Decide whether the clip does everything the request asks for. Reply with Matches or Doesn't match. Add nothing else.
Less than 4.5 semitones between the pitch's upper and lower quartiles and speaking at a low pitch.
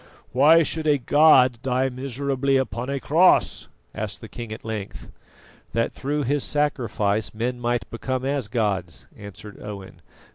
Matches